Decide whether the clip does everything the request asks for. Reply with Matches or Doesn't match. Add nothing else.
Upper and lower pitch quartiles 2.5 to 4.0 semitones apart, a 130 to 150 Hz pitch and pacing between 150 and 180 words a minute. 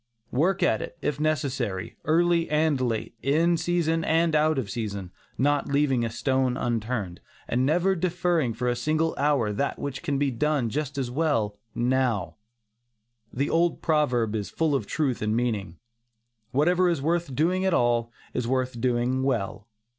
Doesn't match